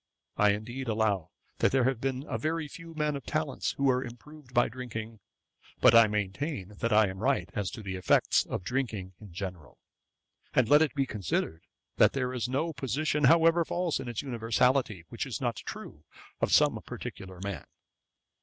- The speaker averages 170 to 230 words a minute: Yes, average, 180 wpm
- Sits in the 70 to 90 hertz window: No, low, 120 Hz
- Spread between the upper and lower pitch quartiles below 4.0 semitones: No, average, 5.0 semitones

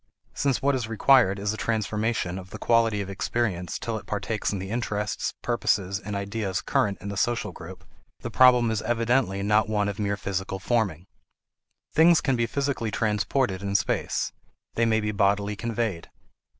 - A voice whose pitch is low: Yes, low, 105 Hz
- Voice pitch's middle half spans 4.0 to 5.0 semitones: No, average, 2.9 semitones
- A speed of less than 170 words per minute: No, average, 175 wpm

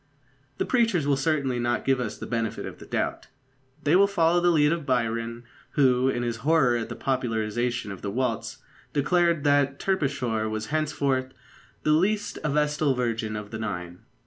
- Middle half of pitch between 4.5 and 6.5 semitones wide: Yes, average, 4.8 semitones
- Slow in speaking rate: No, average, 175 wpm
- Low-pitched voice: Yes, low, 130 Hz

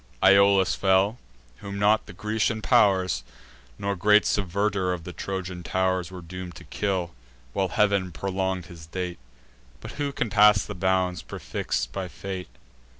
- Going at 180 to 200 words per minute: No, average, 150 wpm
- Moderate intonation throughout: No, narrow, 1.9 semitones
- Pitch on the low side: Yes, very low, 95 Hz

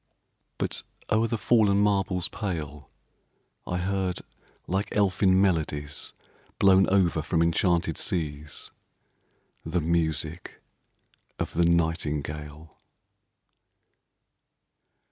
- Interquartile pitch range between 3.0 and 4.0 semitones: Yes, average, 3.6 semitones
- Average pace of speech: No, slow, 85 wpm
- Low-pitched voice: Yes, very low, 85 Hz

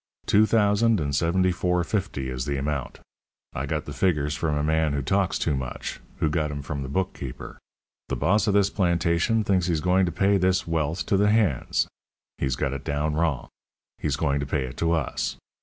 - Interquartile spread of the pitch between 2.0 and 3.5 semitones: No, average, 4.8 semitones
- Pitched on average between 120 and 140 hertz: No, very low, 80 Hz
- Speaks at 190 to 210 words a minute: Yes, fast, 205 wpm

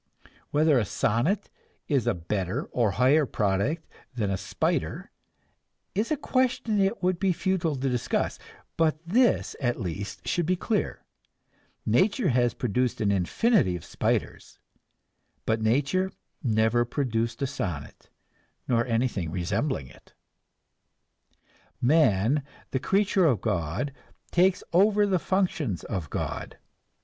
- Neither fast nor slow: No, slow, 125 wpm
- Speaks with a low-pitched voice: Yes, low, 130 Hz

